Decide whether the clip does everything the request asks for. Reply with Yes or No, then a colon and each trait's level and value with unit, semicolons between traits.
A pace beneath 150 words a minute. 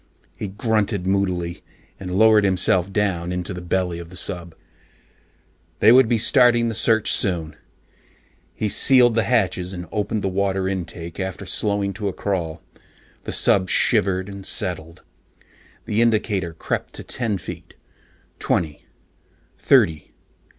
Yes: slow, 135 wpm